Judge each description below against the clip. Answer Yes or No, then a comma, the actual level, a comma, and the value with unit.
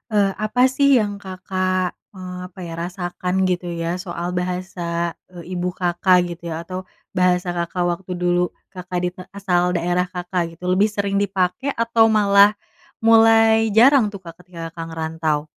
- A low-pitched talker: No, medium, 180 Hz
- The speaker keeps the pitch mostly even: Yes, narrow, 2.3 semitones